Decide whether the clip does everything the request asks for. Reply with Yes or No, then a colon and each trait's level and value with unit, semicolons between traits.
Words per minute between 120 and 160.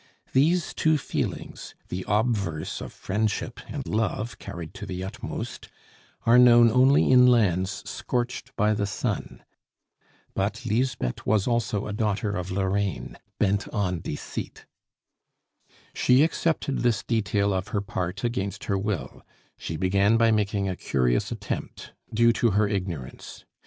Yes: slow, 135 wpm